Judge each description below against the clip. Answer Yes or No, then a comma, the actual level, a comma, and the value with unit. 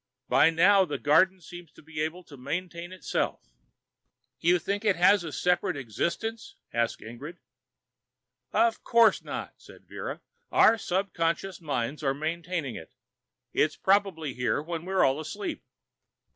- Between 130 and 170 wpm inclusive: Yes, average, 140 wpm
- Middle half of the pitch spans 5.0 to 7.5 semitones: No, average, 4.0 semitones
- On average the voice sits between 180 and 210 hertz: No, medium, 170 Hz